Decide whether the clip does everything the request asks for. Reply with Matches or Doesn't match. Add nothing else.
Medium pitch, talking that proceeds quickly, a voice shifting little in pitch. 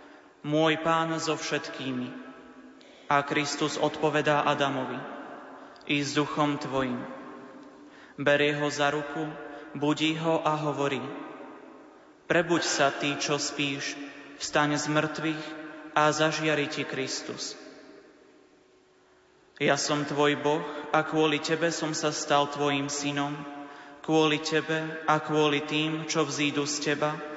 Doesn't match